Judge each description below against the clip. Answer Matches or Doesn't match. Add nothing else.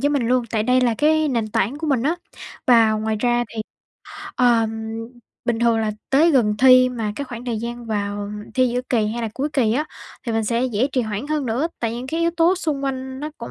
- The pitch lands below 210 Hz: Doesn't match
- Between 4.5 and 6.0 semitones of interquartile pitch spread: Doesn't match